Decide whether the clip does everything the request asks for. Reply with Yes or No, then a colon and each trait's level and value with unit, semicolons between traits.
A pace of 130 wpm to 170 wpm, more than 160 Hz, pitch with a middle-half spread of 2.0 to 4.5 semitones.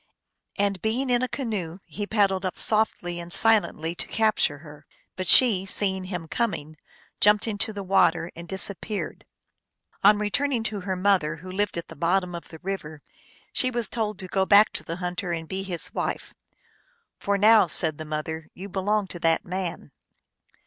No: average, 190 wpm; high, 190 Hz; average, 3.6 semitones